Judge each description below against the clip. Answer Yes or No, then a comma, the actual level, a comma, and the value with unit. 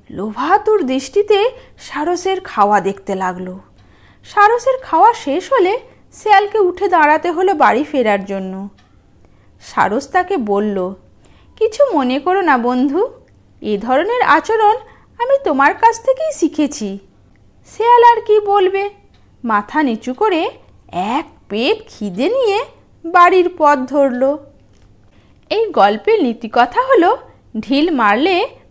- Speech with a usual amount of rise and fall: No, wide, 9.0 semitones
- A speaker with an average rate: Yes, average, 110 wpm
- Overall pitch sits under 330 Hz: No, very high, 335 Hz